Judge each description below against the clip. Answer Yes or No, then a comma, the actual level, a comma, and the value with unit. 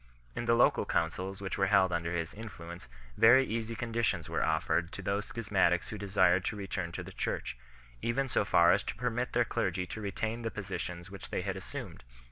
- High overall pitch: No, low, 100 Hz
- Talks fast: Yes, fast, 210 wpm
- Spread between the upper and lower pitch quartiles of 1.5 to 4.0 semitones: No, average, 4.4 semitones